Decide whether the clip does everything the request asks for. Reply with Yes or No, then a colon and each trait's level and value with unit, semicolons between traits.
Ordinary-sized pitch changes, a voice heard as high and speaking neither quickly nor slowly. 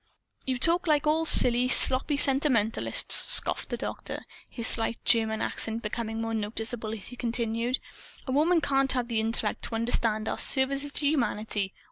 Yes: average, 3.5 semitones; high, 240 Hz; average, 160 wpm